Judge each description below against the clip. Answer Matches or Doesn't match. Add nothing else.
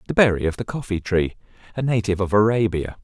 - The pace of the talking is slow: Doesn't match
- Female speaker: Doesn't match